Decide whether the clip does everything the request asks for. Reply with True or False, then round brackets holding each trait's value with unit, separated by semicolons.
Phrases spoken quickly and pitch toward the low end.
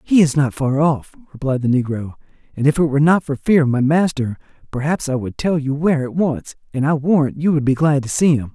False (255 wpm; 145 Hz)